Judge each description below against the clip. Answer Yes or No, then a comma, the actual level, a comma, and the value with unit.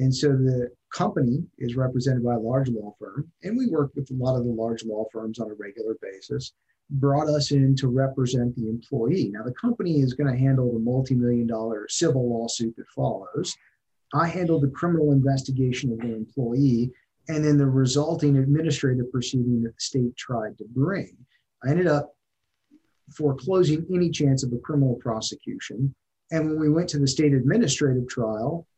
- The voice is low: Yes, low, 130 Hz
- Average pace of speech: Yes, average, 180 wpm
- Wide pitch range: No, average, 3.6 semitones